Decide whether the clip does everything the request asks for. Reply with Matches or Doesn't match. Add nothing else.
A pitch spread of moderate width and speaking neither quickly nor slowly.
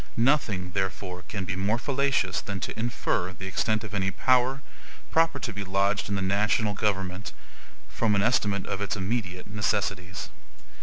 Matches